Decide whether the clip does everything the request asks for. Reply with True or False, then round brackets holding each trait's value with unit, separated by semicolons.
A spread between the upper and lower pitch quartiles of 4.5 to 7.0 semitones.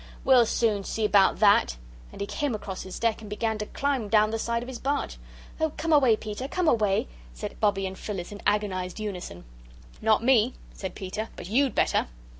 False (3.3 semitones)